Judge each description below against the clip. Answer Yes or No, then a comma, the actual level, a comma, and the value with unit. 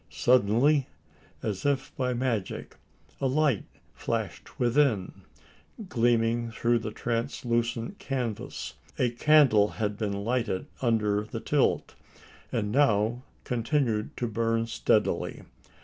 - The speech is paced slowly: Yes, slow, 110 wpm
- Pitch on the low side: Yes, low, 115 Hz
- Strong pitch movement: No, average, 2.8 semitones